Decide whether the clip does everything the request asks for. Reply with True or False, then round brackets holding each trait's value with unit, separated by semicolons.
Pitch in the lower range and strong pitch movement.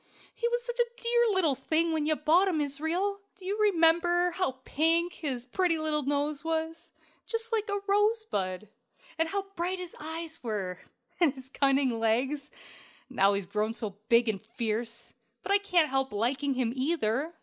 False (315 Hz; 6.1 semitones)